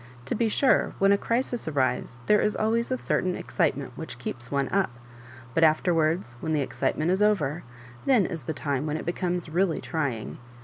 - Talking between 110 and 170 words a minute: No, average, 185 wpm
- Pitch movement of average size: No, wide, 5.8 semitones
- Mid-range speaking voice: Yes, medium, 165 Hz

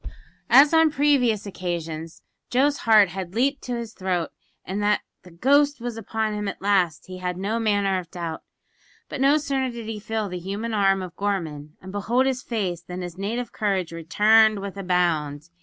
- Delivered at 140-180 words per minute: No, average, 190 wpm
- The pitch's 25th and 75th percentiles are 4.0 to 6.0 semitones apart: Yes, average, 4.4 semitones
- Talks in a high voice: Yes, high, 200 Hz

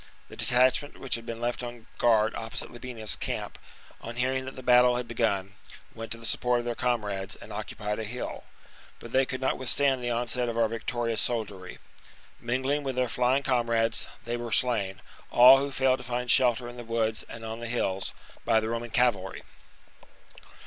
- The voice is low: Yes, low, 120 Hz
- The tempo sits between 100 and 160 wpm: No, average, 195 wpm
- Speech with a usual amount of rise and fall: No, narrow, 1.7 semitones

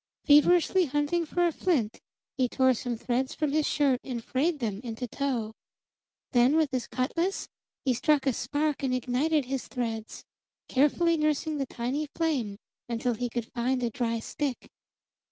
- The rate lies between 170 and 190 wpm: No, average, 160 wpm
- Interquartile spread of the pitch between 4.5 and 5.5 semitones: No, average, 3.8 semitones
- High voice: Yes, very high, 265 Hz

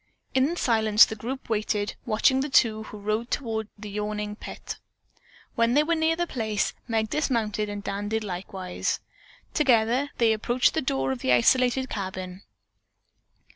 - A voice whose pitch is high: Yes, high, 220 Hz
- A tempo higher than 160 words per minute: No, average, 155 wpm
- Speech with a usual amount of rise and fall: Yes, average, 3.5 semitones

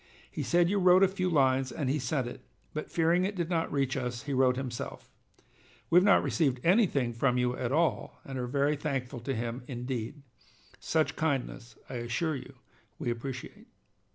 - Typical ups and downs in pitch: Yes, average, 4.7 semitones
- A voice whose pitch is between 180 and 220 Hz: No, low, 135 Hz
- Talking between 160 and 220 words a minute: Yes, average, 185 wpm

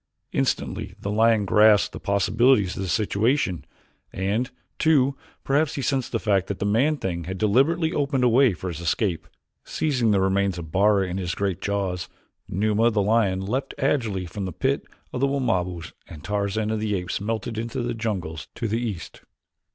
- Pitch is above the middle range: No, low, 105 Hz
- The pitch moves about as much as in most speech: Yes, average, 4.1 semitones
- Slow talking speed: No, average, 180 wpm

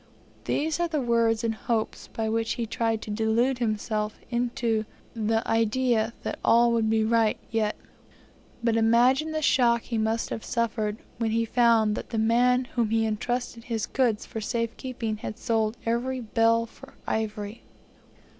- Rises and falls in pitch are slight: Yes, narrow, 1.4 semitones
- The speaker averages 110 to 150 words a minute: No, average, 165 wpm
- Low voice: No, high, 230 Hz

